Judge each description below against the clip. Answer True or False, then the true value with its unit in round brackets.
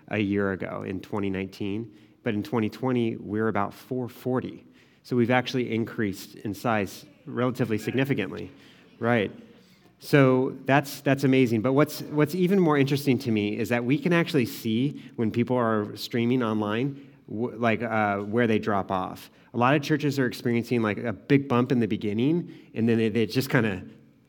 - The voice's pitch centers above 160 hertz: False (120 Hz)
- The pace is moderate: True (170 wpm)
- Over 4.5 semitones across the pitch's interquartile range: False (3.8 semitones)